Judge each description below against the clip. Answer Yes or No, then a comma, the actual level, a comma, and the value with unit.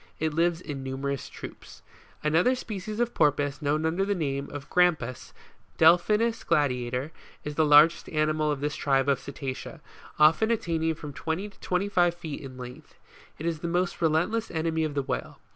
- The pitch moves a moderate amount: Yes, average, 3.5 semitones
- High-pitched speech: No, medium, 155 Hz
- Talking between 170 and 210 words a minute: Yes, average, 175 wpm